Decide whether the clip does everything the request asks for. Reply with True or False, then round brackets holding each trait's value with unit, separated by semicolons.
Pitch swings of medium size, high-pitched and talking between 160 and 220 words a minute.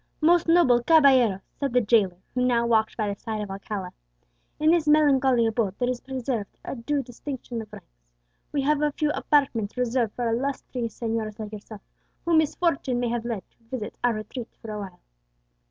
True (4.2 semitones; 240 Hz; 185 wpm)